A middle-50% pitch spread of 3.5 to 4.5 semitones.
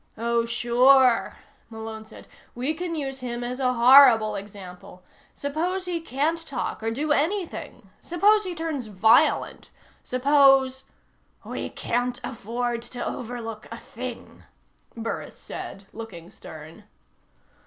Yes: average, 4.2 semitones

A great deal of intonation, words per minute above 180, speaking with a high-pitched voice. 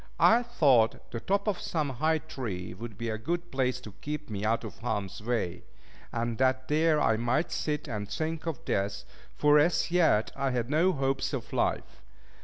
No: wide, 5.8 semitones; average, 190 wpm; low, 130 Hz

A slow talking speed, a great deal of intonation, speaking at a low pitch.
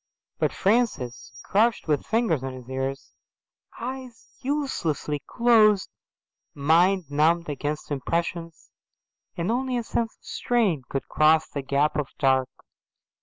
No: slow, 120 wpm; wide, 8.0 semitones; medium, 165 Hz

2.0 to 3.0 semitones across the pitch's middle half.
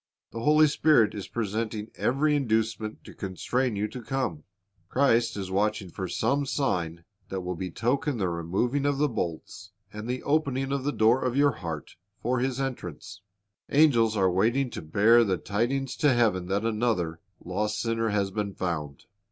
No: wide, 5.4 semitones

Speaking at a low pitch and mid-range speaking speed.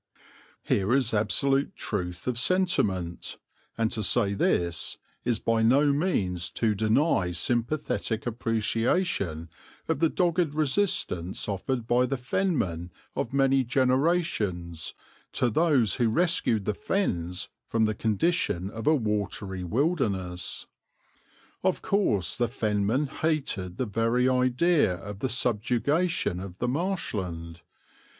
No: low, 115 Hz; slow, 120 wpm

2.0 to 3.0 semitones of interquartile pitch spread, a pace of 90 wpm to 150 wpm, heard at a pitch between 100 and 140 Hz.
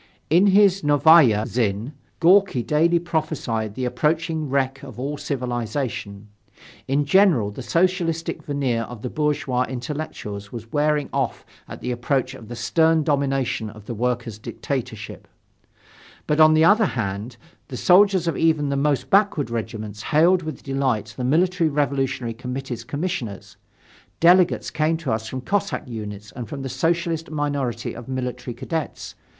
No: average, 5.1 semitones; average, 145 wpm; low, 135 Hz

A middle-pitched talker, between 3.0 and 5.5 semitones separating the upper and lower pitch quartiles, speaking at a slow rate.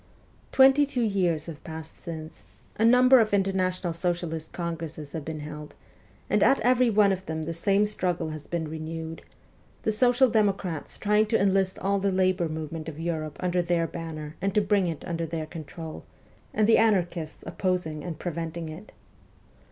No: medium, 175 Hz; average, 3.8 semitones; average, 170 wpm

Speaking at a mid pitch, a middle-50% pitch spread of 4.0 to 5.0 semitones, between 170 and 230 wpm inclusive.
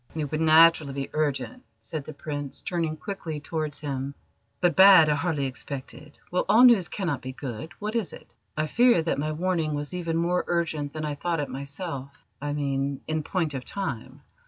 No: medium, 155 Hz; average, 3.5 semitones; average, 190 wpm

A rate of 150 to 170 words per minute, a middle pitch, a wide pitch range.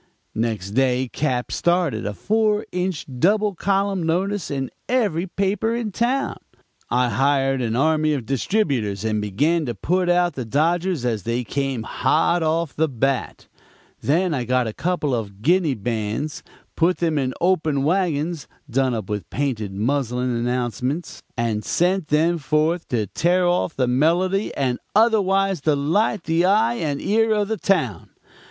Yes: average, 155 wpm; medium, 150 Hz; wide, 6.6 semitones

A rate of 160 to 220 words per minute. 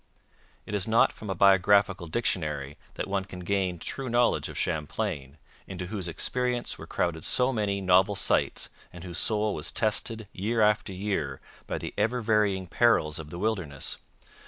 Yes: average, 165 wpm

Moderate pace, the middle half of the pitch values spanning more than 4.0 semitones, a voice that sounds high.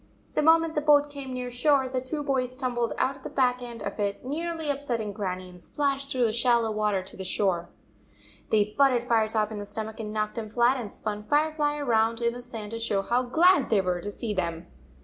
No: fast, 225 wpm; average, 4.5 semitones; high, 240 Hz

